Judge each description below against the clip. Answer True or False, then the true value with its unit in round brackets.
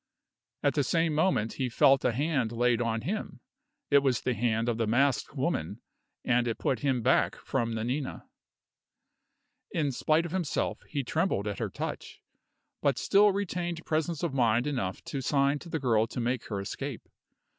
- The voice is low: True (130 Hz)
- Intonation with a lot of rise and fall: False (4.8 semitones)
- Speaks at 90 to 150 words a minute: False (175 wpm)